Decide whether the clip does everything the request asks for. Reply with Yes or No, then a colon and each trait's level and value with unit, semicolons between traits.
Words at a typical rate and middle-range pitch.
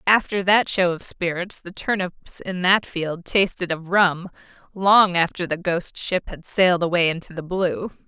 Yes: average, 180 wpm; medium, 180 Hz